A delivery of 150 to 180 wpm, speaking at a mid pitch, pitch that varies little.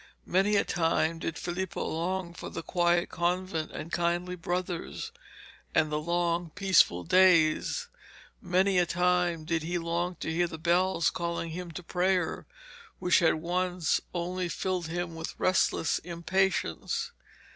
No: average, 140 wpm; medium, 175 Hz; narrow, 1.6 semitones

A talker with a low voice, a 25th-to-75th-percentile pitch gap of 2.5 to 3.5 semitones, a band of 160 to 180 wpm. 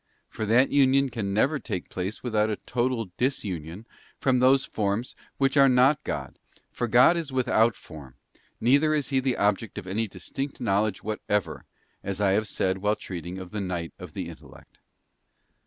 No: low, 110 Hz; average, 5.0 semitones; average, 170 wpm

